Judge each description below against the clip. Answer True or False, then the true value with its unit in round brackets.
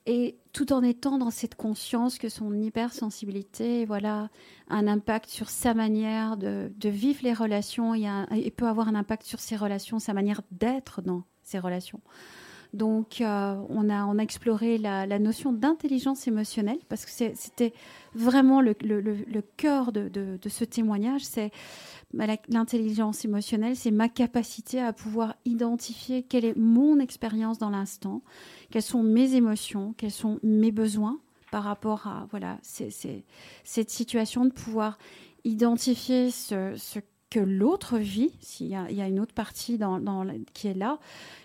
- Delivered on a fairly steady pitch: True (2.3 semitones)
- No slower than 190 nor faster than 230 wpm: False (170 wpm)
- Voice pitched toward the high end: True (220 Hz)